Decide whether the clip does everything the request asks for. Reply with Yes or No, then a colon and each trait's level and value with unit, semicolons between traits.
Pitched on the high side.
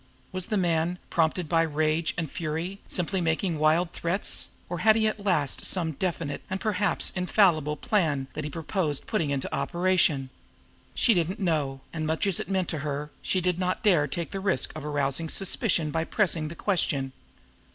No: medium, 165 Hz